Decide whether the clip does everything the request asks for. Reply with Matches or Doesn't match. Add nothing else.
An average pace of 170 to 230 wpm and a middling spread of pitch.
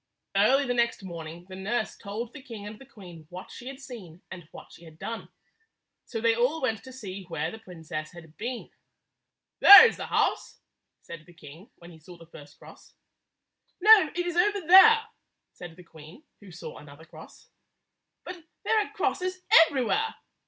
Doesn't match